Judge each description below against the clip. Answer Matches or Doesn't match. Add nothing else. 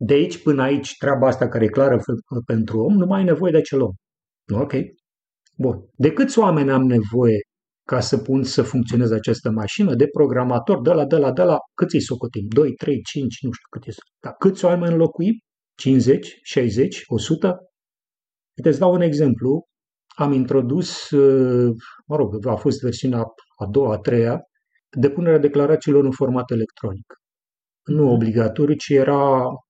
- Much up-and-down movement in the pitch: Doesn't match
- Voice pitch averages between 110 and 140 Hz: Matches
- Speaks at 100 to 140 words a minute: Doesn't match